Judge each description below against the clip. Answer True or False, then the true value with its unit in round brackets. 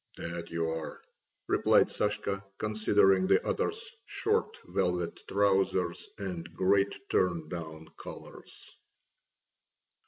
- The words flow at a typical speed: False (90 wpm)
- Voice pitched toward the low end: True (95 Hz)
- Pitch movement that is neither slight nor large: True (3.2 semitones)